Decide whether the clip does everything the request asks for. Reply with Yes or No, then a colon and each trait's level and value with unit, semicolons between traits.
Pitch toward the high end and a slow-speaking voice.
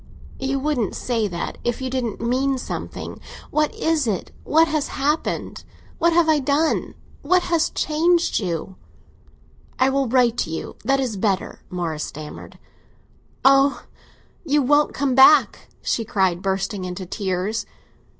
Yes: very high, 260 Hz; slow, 130 wpm